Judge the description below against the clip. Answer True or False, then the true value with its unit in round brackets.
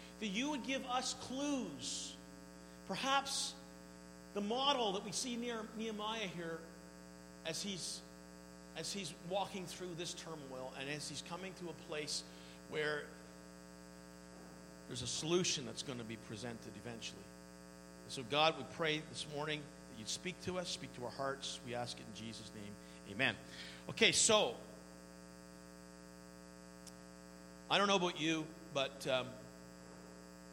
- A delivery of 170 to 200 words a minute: False (140 wpm)